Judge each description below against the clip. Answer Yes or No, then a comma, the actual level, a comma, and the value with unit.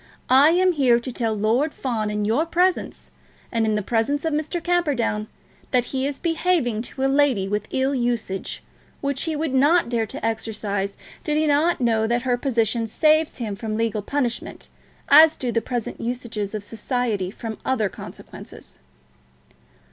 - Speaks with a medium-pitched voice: No, high, 245 Hz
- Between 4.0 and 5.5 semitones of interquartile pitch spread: Yes, average, 4.7 semitones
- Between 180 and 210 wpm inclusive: No, average, 170 wpm